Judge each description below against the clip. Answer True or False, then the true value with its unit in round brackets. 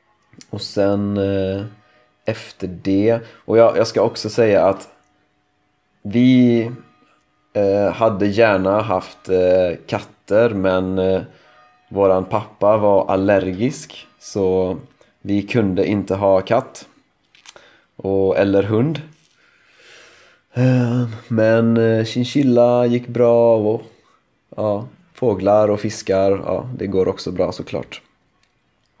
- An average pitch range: True (3.2 semitones)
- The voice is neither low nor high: False (105 Hz)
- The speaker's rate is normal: False (105 wpm)